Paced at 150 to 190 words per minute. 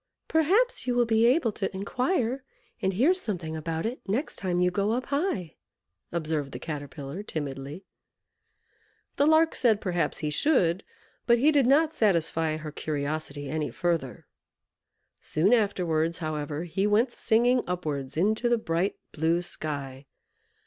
No: average, 140 wpm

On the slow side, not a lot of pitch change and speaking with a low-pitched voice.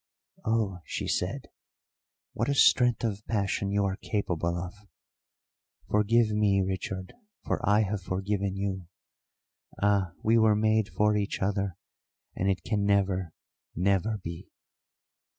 Yes: slow, 130 wpm; narrow, 2.0 semitones; low, 100 Hz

